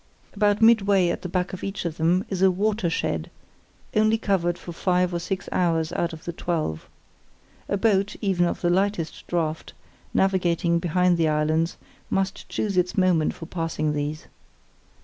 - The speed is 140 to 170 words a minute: Yes, average, 165 wpm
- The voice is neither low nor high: Yes, medium, 180 Hz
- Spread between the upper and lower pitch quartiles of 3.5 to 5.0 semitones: No, average, 2.7 semitones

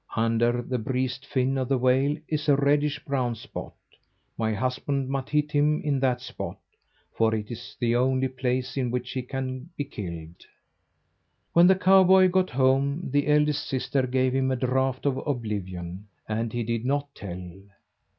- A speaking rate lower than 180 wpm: Yes, average, 170 wpm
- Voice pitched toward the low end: Yes, low, 130 Hz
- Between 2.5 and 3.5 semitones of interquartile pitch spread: Yes, average, 2.9 semitones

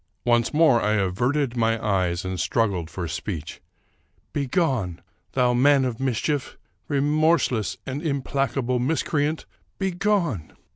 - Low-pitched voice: Yes, low, 125 Hz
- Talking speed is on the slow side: Yes, slow, 130 wpm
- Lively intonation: Yes, wide, 5.9 semitones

